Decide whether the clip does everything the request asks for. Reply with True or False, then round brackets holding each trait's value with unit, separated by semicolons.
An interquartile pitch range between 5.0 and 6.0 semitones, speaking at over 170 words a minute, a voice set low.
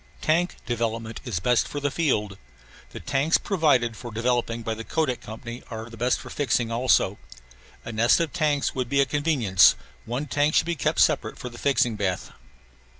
False (4.1 semitones; 180 wpm; 125 Hz)